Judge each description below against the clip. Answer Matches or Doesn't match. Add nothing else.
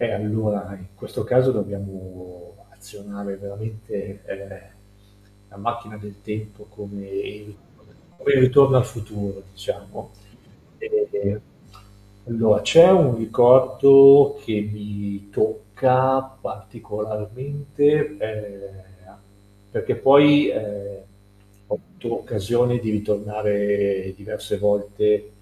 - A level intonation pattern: Doesn't match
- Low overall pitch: Matches